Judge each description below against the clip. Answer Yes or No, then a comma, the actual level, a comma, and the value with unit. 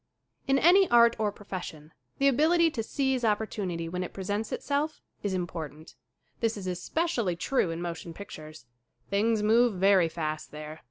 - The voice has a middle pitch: No, high, 200 Hz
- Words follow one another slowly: No, average, 160 wpm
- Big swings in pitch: Yes, wide, 6.0 semitones